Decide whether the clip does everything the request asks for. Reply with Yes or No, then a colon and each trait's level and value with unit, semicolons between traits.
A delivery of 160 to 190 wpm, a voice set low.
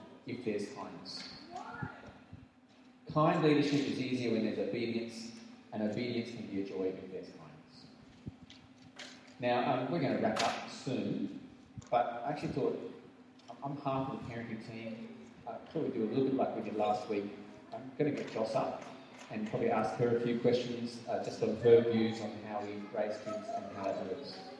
Yes: average, 185 wpm; low, 115 Hz